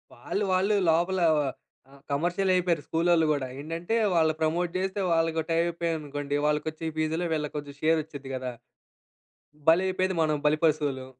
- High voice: No, medium, 160 Hz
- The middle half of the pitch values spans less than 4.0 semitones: Yes, average, 2.7 semitones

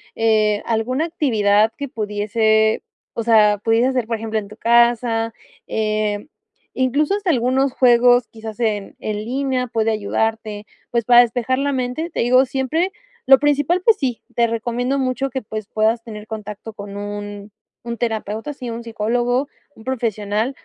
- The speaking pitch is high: Yes, high, 230 Hz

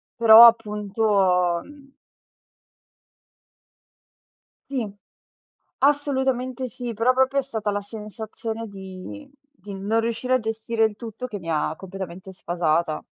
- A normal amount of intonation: Yes, average, 4.5 semitones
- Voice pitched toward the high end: Yes, high, 220 Hz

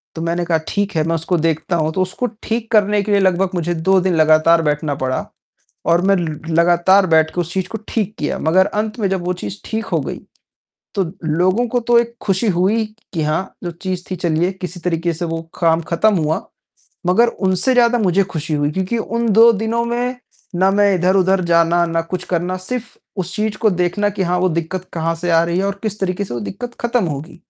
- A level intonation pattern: No, average, 3.6 semitones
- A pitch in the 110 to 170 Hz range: No, medium, 180 Hz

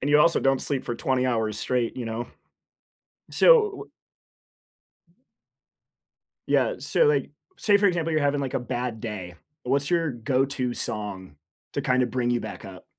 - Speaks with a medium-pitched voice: No, low, 130 Hz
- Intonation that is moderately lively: Yes, average, 3.7 semitones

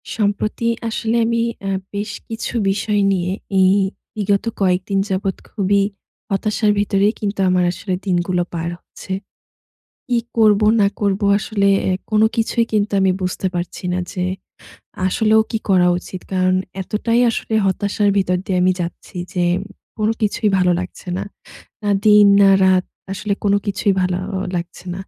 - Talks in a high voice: Yes, high, 200 Hz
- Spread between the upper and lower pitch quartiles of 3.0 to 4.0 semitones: No, narrow, 2.4 semitones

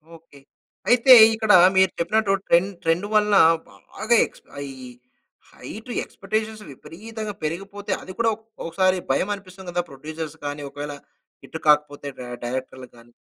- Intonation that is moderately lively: No, wide, 5.9 semitones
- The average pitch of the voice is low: No, medium, 185 Hz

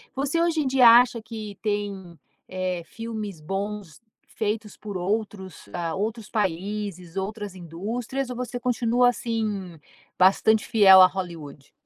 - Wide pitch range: No, average, 3.6 semitones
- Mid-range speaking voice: No, high, 210 Hz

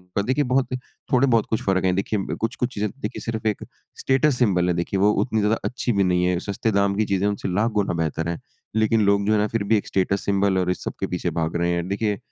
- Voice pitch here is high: No, low, 100 Hz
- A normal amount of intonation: Yes, average, 3.2 semitones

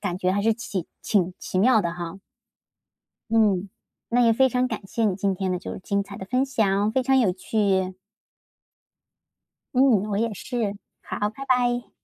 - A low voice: No, high, 210 Hz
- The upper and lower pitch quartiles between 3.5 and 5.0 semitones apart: Yes, average, 4.2 semitones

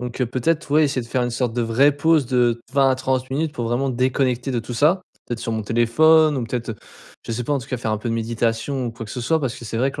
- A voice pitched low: Yes, low, 125 Hz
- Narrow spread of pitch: No, average, 3.0 semitones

